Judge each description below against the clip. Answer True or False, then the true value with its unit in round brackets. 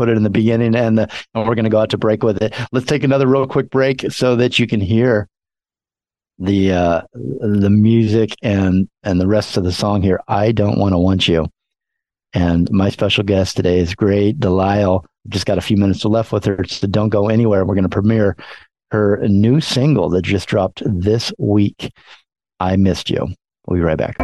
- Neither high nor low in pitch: False (105 Hz)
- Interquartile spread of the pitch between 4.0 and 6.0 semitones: False (3.0 semitones)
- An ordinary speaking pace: False (210 wpm)